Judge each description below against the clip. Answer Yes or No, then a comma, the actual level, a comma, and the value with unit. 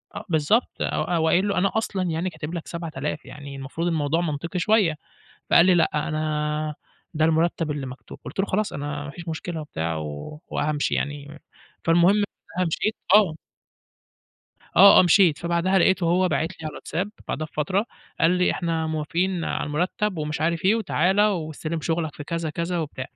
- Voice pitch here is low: No, medium, 165 Hz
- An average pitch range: Yes, average, 3.1 semitones